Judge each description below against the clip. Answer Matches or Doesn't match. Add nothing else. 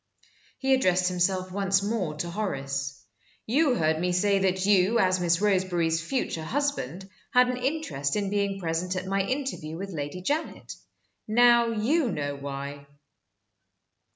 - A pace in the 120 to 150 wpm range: Matches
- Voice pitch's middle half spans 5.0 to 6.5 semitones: Matches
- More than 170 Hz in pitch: Matches